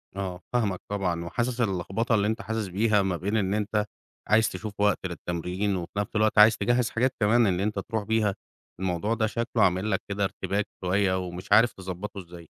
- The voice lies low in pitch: Yes, low, 100 Hz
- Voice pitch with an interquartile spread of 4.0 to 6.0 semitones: No, average, 3.0 semitones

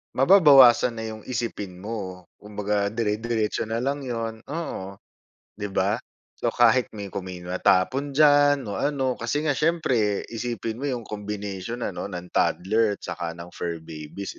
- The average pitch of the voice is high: No, low, 110 Hz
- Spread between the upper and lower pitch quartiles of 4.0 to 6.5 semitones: Yes, average, 4.4 semitones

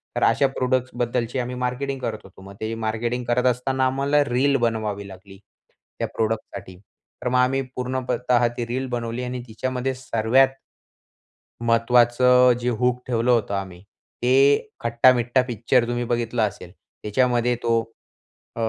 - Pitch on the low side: Yes, low, 120 Hz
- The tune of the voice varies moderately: No, narrow, 1.8 semitones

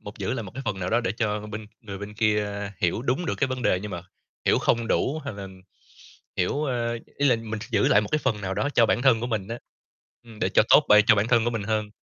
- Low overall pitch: Yes, low, 110 Hz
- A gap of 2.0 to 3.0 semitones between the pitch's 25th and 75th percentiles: Yes, average, 2.7 semitones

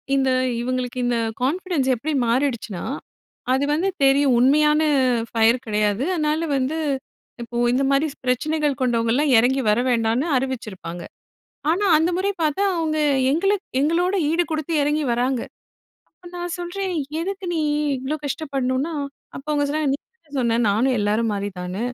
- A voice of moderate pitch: No, very high, 275 Hz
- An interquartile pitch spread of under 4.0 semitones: No, average, 4.7 semitones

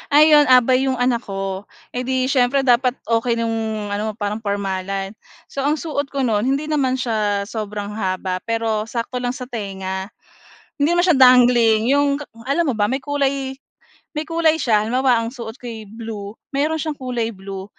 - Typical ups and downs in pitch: Yes, average, 4.3 semitones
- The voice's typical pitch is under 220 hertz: No, high, 240 Hz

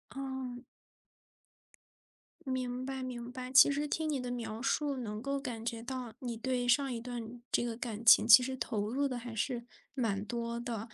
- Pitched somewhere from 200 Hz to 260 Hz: Yes, high, 245 Hz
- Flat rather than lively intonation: Yes, narrow, 2.1 semitones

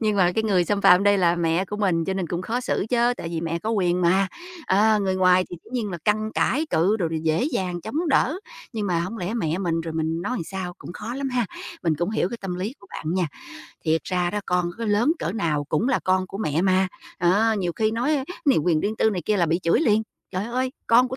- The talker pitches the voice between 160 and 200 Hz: Yes, high, 190 Hz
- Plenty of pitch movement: No, average, 4.2 semitones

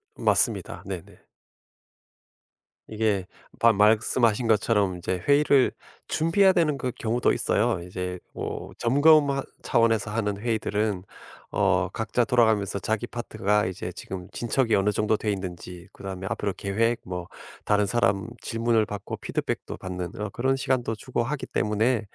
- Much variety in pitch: No, average, 3.4 semitones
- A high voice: No, low, 110 Hz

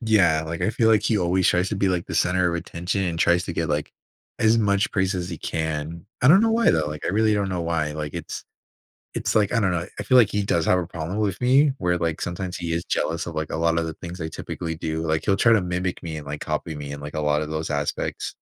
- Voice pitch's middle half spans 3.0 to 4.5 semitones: Yes, average, 3.8 semitones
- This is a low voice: Yes, very low, 85 Hz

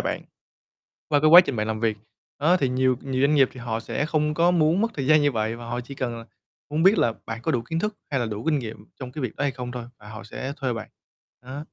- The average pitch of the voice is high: No, low, 130 Hz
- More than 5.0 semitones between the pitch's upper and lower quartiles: No, average, 4.5 semitones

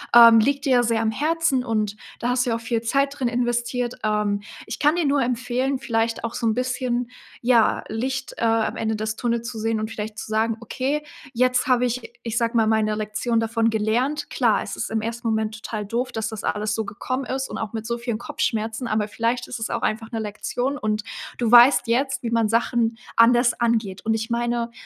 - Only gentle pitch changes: Yes, narrow, 2.1 semitones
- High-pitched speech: Yes, high, 230 Hz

